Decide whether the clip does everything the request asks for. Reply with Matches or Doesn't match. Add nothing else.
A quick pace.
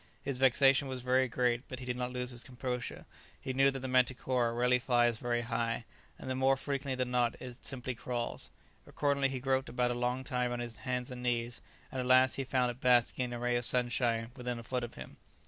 Matches